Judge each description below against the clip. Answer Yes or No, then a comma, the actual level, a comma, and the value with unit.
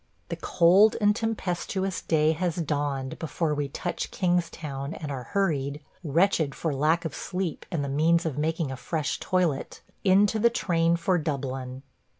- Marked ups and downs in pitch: No, average, 4.0 semitones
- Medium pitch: Yes, medium, 165 Hz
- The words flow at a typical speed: Yes, average, 165 wpm